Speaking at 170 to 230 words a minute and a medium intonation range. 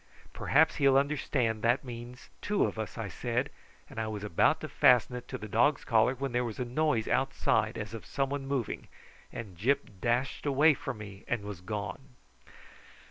Yes: average, 190 wpm; average, 3.9 semitones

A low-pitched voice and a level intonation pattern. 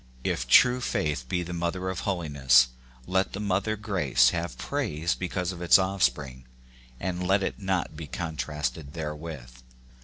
No: very low, 85 Hz; average, 5.1 semitones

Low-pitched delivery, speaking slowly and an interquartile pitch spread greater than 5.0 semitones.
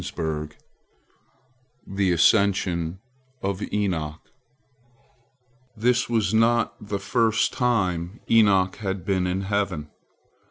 No: low, 100 Hz; slow, 85 wpm; average, 3.4 semitones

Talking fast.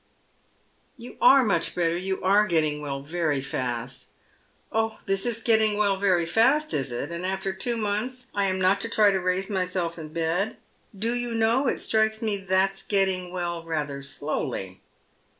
No: average, 185 wpm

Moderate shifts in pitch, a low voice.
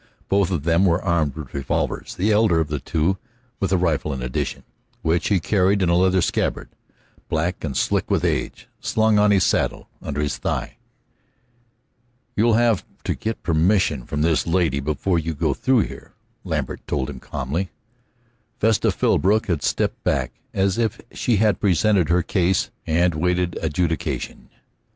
Yes: average, 4.0 semitones; very low, 90 Hz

